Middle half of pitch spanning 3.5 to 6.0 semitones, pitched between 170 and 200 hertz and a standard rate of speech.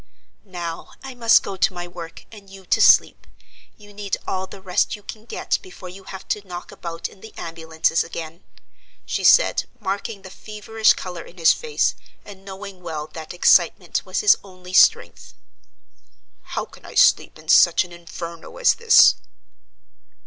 No: average, 3.1 semitones; high, 190 Hz; average, 170 wpm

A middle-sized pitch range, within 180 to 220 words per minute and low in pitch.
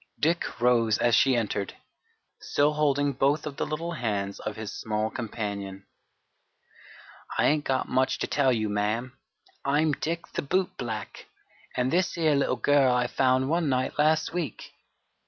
No: average, 4.9 semitones; average, 155 wpm; low, 130 Hz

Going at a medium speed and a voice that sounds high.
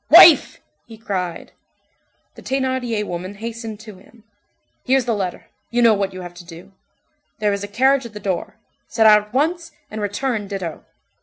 Yes: average, 175 wpm; high, 210 Hz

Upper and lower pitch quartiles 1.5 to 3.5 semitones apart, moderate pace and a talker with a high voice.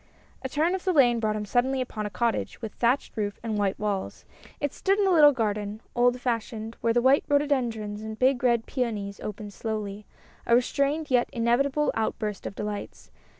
No: average, 3.9 semitones; average, 195 wpm; high, 235 Hz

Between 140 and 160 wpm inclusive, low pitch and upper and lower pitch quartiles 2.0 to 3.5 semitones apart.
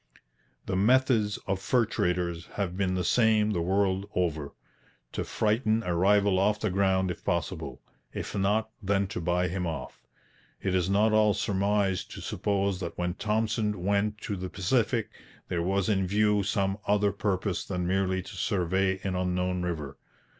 No: average, 170 wpm; very low, 95 Hz; narrow, 2.4 semitones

